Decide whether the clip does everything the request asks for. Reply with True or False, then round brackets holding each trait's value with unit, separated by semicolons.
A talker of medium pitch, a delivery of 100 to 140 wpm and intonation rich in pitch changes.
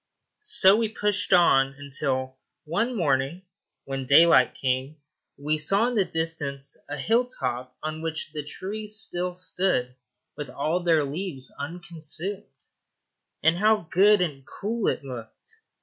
True (165 Hz; 135 wpm; 6.1 semitones)